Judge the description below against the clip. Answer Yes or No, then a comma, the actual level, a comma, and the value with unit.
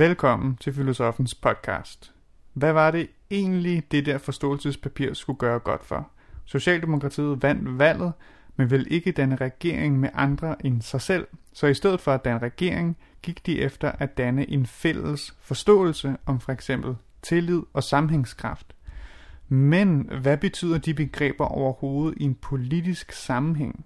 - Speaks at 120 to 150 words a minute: Yes, slow, 145 wpm